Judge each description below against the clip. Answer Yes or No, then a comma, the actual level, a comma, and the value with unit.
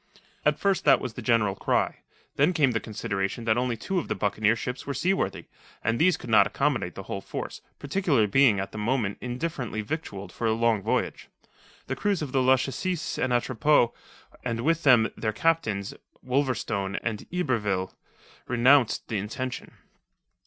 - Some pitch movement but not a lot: Yes, average, 4.6 semitones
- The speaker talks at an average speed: Yes, average, 165 wpm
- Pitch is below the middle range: Yes, low, 120 Hz